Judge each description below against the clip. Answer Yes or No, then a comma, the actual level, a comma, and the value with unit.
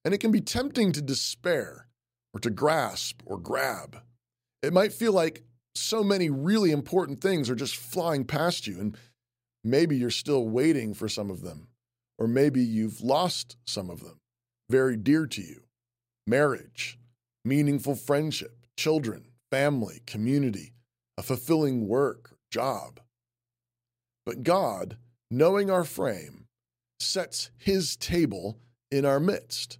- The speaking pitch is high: No, low, 125 Hz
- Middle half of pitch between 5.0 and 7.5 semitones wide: No, average, 4.2 semitones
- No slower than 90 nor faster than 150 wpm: Yes, slow, 135 wpm